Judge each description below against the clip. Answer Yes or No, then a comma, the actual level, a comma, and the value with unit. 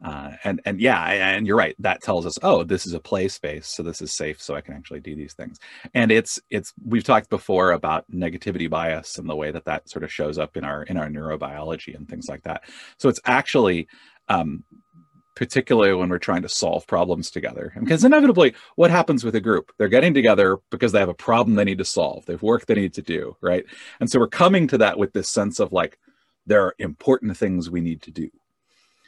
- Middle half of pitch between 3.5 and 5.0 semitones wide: No, wide, 5.5 semitones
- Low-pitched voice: Yes, very low, 95 Hz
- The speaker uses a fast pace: Yes, fast, 230 wpm